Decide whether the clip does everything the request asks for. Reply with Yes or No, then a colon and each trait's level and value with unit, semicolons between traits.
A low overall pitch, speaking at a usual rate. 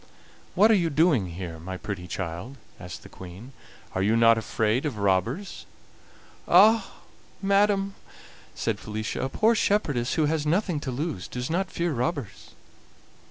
Yes: low, 130 Hz; average, 150 wpm